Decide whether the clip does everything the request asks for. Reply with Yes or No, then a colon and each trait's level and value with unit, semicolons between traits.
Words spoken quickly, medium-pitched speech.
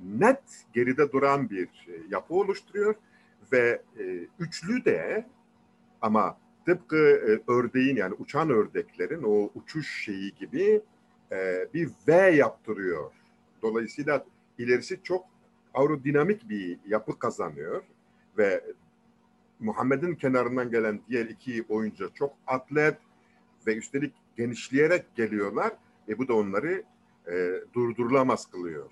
No: average, 110 wpm; medium, 155 Hz